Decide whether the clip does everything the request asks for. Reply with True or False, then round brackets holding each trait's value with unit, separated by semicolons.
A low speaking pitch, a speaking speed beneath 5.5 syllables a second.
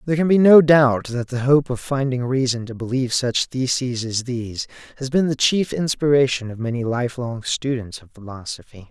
True (130 Hz; 5.2 syllables/s)